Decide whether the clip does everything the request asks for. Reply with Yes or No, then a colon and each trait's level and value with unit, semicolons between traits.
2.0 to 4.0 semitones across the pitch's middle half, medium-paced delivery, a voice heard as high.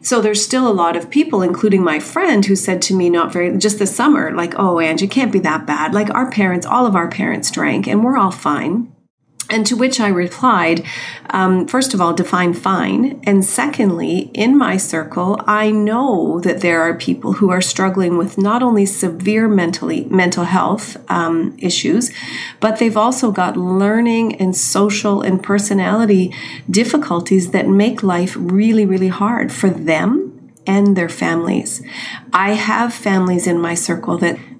Yes: average, 3.5 semitones; average, 175 wpm; high, 195 Hz